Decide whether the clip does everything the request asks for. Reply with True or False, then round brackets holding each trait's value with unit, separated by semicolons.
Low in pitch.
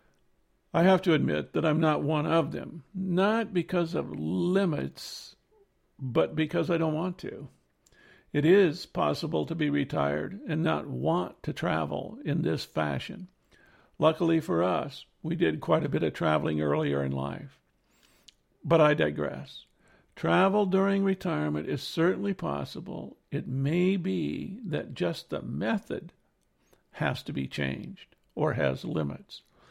False (160 Hz)